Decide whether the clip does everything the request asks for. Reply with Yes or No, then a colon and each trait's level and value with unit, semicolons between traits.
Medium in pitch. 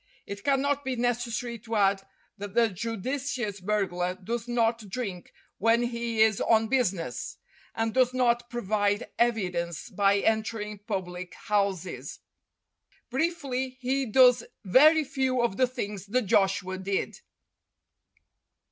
No: high, 225 Hz